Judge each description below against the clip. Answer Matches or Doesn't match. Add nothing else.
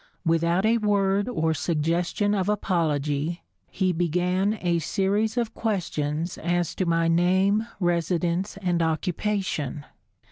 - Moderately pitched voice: Matches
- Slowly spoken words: Matches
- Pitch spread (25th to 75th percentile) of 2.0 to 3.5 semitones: Matches